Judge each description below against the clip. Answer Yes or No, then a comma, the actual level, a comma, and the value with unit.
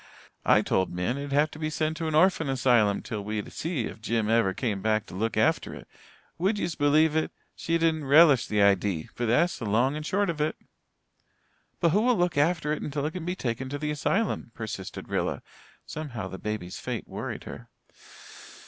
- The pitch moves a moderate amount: No, wide, 6.4 semitones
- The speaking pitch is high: No, medium, 145 Hz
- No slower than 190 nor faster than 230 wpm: Yes, average, 200 wpm